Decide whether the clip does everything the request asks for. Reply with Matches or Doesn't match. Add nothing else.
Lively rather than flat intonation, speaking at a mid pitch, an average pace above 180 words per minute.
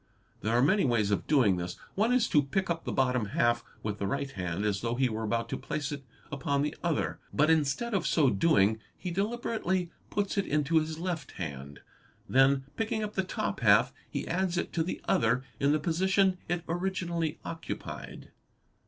Matches